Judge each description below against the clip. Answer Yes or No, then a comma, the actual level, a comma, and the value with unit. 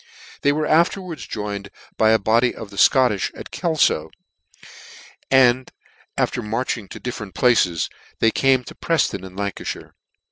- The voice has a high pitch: No, low, 120 Hz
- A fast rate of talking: No, average, 140 wpm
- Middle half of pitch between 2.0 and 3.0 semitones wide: No, average, 4.8 semitones